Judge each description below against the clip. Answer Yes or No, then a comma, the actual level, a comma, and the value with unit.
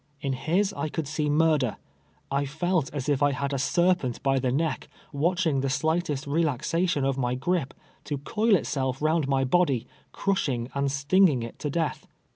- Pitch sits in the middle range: Yes, medium, 145 Hz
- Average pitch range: Yes, average, 3.6 semitones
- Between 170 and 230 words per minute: Yes, average, 185 wpm